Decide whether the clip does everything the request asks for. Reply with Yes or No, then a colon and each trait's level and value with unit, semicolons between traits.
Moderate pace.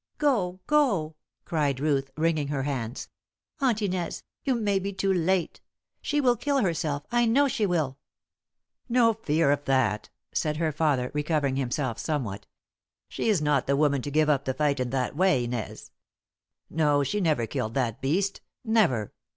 Yes: average, 165 wpm